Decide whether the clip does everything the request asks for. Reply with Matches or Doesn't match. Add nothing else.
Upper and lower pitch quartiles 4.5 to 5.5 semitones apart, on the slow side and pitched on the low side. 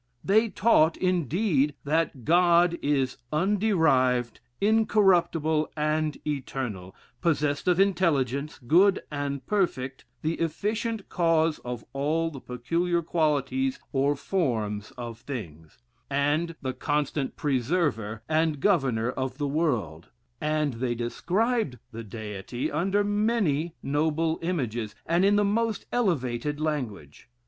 Doesn't match